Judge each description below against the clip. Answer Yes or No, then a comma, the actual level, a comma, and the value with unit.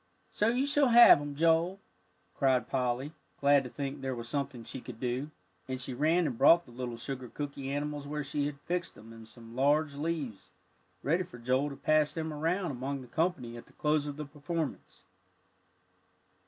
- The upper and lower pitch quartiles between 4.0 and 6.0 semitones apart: No, average, 3.5 semitones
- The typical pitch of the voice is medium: Yes, medium, 145 Hz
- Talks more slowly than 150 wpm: No, average, 190 wpm